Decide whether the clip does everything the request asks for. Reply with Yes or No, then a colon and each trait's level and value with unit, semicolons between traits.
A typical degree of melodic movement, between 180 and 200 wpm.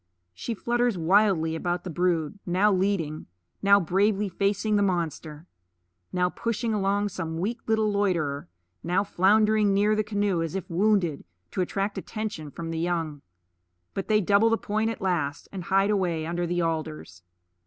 No: average, 3.7 semitones; average, 160 wpm